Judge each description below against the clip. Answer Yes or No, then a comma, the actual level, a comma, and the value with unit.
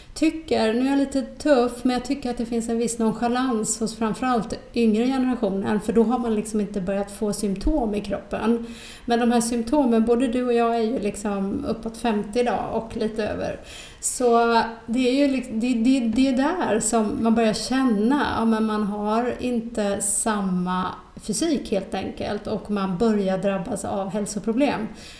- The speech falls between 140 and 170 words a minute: No, average, 180 wpm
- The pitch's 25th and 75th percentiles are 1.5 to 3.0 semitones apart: Yes, average, 2.7 semitones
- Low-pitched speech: No, high, 230 Hz